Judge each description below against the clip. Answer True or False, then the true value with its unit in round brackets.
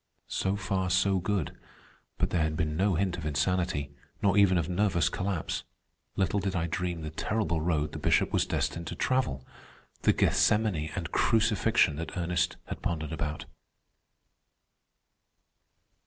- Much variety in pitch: False (3.7 semitones)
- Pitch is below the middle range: True (90 Hz)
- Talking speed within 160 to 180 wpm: False (140 wpm)